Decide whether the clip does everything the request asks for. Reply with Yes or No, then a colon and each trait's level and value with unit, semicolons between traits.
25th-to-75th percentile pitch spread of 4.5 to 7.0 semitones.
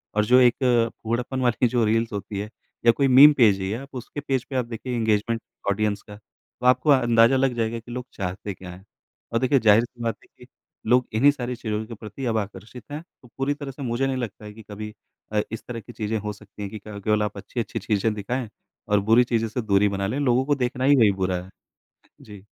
No: average, 3.2 semitones